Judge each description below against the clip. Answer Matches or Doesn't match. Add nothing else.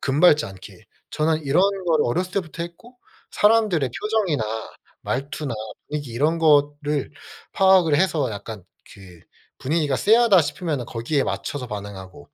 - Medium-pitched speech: Matches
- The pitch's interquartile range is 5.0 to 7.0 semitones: Matches